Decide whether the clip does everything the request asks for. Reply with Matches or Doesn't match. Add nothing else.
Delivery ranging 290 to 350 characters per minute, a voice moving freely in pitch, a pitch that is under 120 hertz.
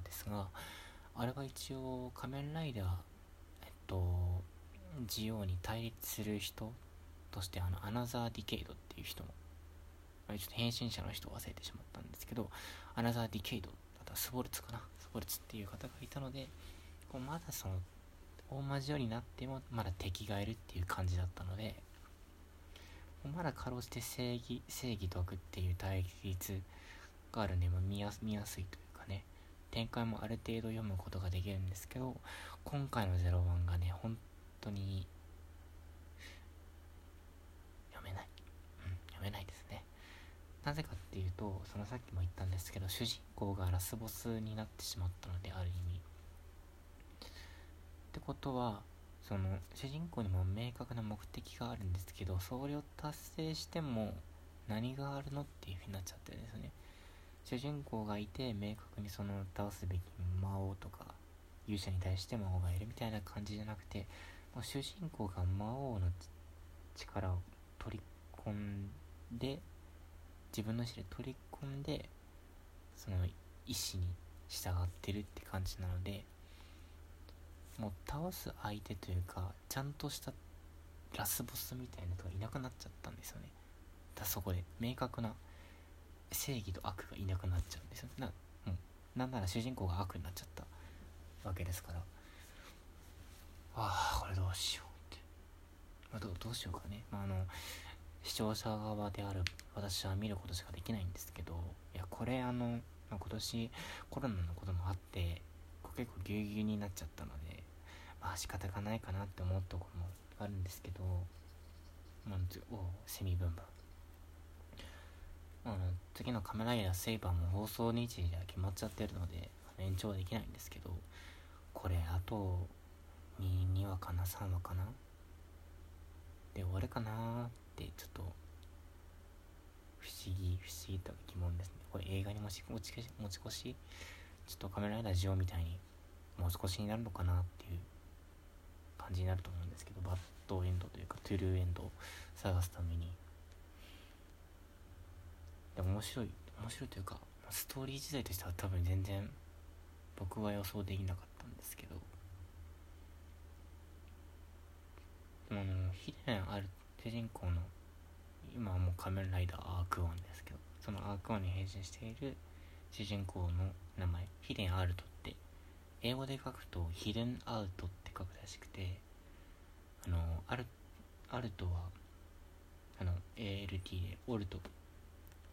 Doesn't match